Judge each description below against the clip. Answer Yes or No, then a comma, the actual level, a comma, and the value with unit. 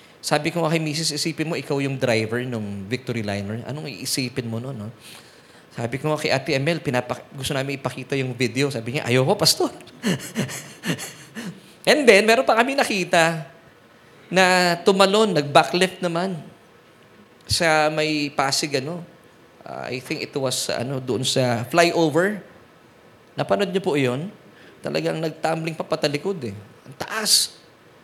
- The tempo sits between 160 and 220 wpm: No, average, 145 wpm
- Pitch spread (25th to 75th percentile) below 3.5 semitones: No, average, 4.7 semitones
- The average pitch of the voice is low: No, medium, 150 Hz